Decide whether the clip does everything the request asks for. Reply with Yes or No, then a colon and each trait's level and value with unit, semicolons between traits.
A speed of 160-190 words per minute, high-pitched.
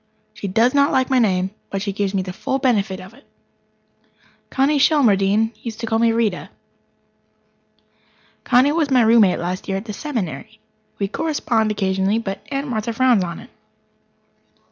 Yes: average, 165 wpm; high, 220 Hz